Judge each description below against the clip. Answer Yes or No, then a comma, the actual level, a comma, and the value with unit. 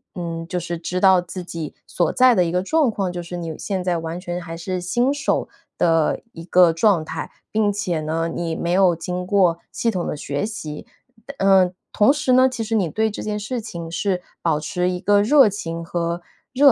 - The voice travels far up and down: No, average, 3.7 semitones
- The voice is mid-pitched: Yes, medium, 180 Hz